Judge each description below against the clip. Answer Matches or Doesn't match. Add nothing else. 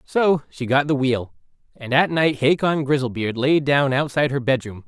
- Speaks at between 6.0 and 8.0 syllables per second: Doesn't match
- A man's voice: Matches